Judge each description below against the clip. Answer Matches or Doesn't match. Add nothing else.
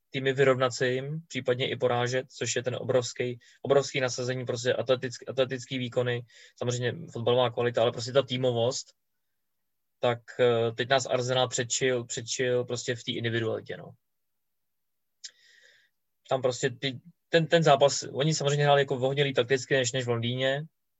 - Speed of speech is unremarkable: Matches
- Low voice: Matches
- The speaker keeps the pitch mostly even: Matches